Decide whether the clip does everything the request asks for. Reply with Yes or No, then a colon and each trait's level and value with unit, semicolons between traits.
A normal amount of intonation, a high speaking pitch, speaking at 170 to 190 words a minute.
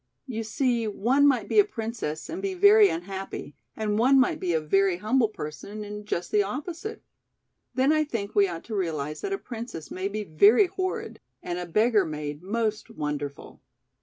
No: wide, 6.5 semitones; high, 215 Hz; average, 185 wpm